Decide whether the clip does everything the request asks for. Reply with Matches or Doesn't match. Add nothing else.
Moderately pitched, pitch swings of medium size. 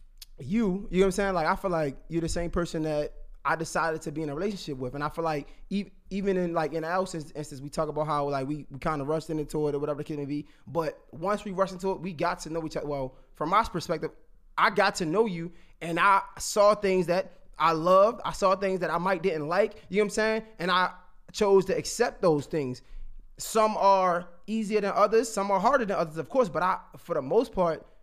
Matches